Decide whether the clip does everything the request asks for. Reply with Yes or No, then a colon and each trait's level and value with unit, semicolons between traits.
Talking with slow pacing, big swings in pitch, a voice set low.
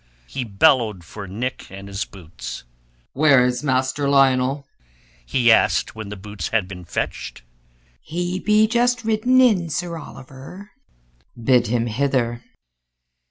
Yes: slow, 130 wpm; wide, 6.8 semitones; low, 130 Hz